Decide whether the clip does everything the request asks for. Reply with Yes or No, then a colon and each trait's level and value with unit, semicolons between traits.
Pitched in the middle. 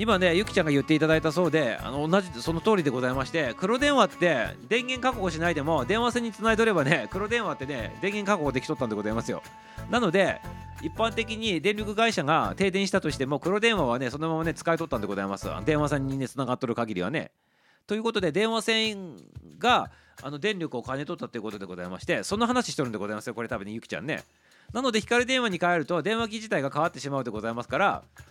Yes: medium, 170 Hz